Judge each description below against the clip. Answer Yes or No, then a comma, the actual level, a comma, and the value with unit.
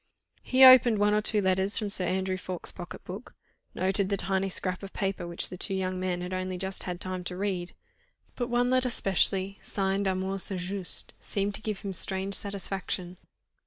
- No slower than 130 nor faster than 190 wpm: No, average, 200 wpm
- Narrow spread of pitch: Yes, narrow, 1.5 semitones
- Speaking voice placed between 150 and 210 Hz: Yes, high, 190 Hz